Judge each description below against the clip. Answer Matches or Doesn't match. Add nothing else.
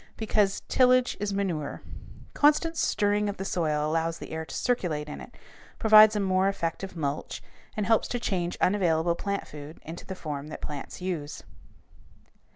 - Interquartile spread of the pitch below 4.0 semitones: Doesn't match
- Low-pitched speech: Doesn't match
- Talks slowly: Doesn't match